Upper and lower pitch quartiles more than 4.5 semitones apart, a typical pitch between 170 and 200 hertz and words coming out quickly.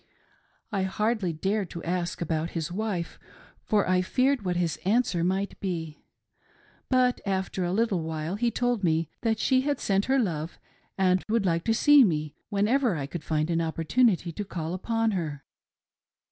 No: average, 4.9 semitones; high, 190 Hz; average, 170 wpm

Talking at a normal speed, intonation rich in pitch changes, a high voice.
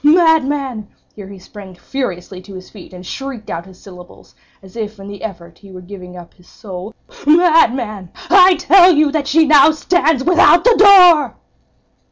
Yes: average, 165 wpm; wide, 9.0 semitones; high, 225 Hz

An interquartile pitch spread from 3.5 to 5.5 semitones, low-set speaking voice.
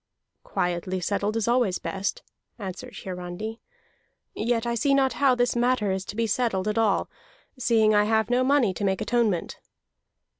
No: average, 3.9 semitones; high, 220 Hz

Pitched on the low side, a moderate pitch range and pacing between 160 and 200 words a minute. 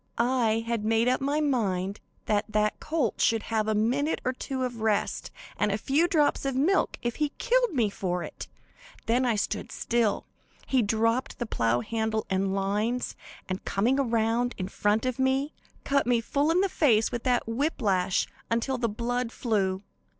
No: high, 230 Hz; average, 3.8 semitones; average, 180 wpm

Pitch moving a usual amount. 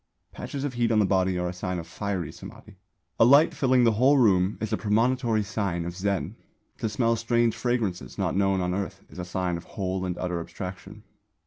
Yes: average, 3.9 semitones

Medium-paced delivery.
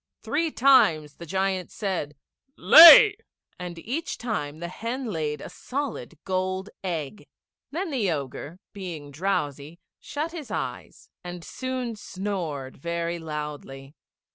No: slow, 120 wpm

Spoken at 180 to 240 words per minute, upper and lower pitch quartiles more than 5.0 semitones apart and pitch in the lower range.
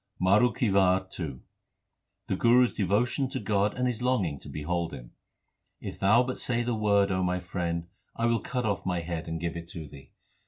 Yes: average, 195 wpm; wide, 5.6 semitones; very low, 95 Hz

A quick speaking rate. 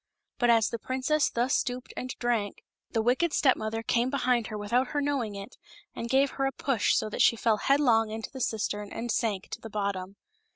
Yes: fast, 210 wpm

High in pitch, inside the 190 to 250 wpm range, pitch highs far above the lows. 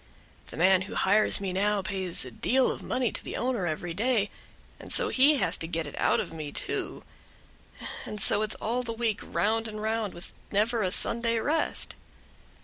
No: high, 215 Hz; average, 195 wpm; average, 3.7 semitones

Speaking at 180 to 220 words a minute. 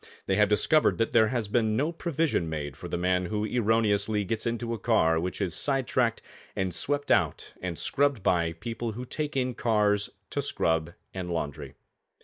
Yes: average, 185 wpm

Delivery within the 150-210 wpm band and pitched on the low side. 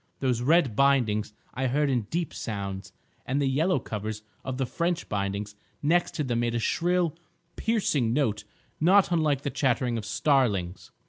Yes: average, 160 wpm; low, 130 Hz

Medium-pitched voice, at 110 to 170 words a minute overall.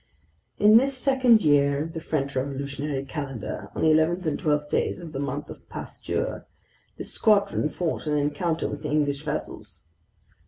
Yes: medium, 150 Hz; average, 160 wpm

